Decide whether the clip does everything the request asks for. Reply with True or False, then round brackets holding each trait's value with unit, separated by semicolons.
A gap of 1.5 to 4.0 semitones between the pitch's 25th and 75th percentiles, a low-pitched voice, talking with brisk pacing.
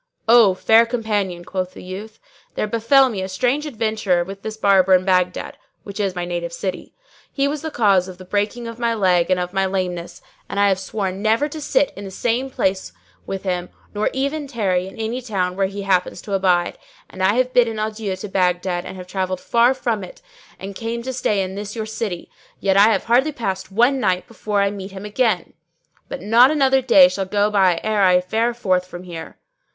False (3.7 semitones; 200 Hz; 210 wpm)